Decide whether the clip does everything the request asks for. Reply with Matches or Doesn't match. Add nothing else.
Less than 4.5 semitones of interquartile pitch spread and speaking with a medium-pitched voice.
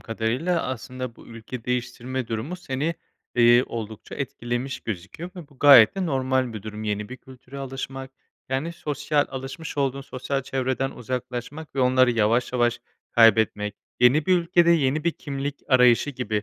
Doesn't match